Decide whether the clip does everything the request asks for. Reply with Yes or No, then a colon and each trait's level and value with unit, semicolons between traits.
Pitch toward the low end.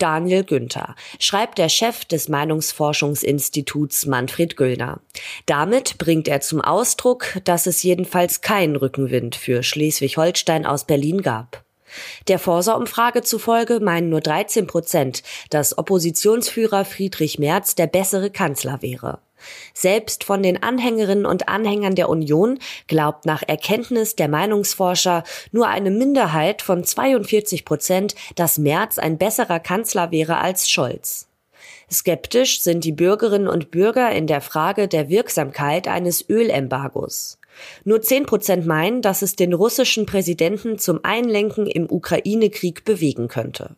No: medium, 180 Hz